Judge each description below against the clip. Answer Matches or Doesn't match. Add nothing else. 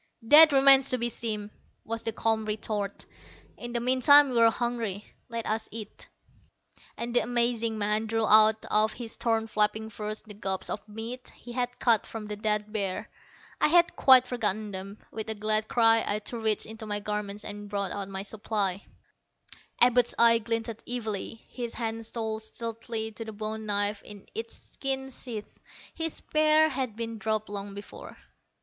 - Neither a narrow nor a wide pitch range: Doesn't match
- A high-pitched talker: Matches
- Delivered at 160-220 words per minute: Matches